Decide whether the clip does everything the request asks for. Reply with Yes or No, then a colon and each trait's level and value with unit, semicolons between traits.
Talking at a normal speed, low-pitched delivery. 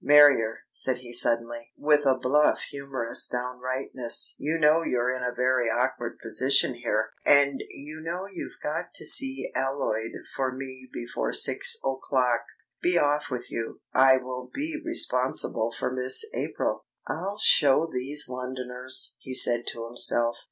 Yes: average, 145 wpm; low, 130 Hz